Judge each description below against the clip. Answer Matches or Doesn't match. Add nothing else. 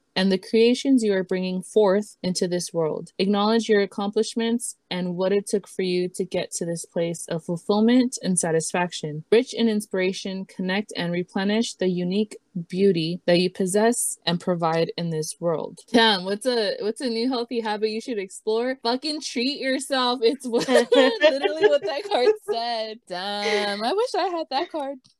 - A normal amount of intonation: Matches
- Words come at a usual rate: Matches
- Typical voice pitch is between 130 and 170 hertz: Doesn't match